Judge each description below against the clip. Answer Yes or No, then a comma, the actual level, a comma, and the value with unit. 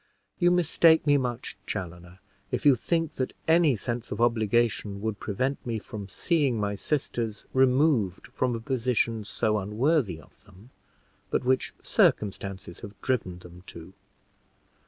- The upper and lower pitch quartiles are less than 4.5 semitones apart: No, average, 4.9 semitones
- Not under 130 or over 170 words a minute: Yes, average, 140 wpm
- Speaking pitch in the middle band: No, low, 115 Hz